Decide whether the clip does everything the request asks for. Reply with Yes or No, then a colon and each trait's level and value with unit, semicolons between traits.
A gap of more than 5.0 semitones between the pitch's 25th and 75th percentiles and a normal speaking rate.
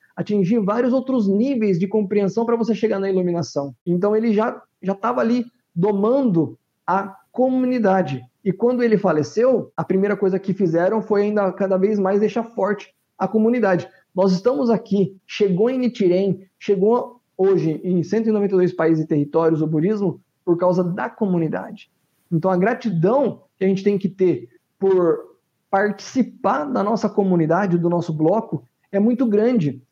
No: average, 3.6 semitones; average, 155 wpm